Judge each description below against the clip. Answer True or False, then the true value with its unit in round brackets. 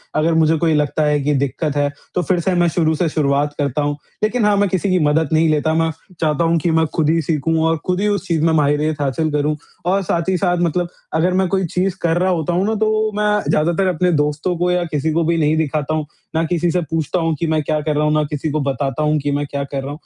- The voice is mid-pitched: True (160 Hz)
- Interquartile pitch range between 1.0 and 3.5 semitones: True (2.9 semitones)